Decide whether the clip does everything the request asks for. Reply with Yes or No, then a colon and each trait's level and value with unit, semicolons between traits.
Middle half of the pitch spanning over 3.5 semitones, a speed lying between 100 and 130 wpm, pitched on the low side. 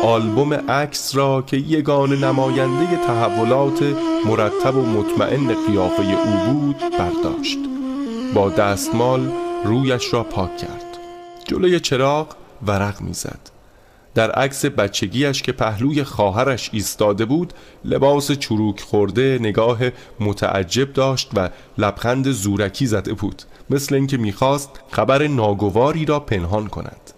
Yes: average, 5.2 semitones; average, 115 wpm; low, 130 Hz